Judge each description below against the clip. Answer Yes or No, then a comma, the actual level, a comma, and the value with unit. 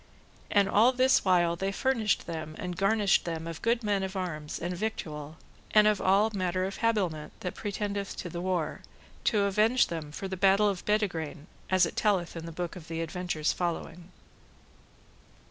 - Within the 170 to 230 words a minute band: Yes, average, 175 wpm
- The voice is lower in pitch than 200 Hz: Yes, medium, 185 Hz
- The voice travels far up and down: No, average, 3.6 semitones